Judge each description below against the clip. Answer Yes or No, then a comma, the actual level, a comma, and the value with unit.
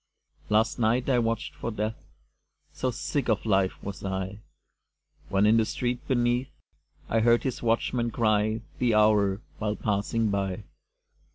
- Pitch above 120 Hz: No, low, 110 Hz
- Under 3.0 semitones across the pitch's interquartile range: Yes, narrow, 2.5 semitones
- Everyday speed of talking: Yes, average, 145 wpm